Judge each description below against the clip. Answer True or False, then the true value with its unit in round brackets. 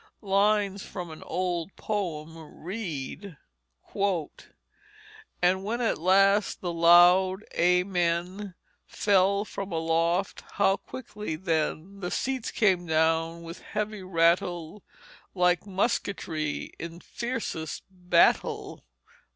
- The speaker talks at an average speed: False (95 wpm)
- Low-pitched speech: False (180 Hz)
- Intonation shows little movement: False (3.1 semitones)